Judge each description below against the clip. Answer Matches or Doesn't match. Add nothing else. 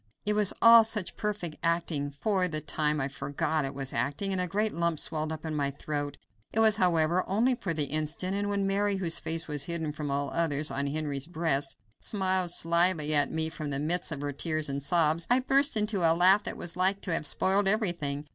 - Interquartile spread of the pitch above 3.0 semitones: Matches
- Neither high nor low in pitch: Matches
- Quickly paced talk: Matches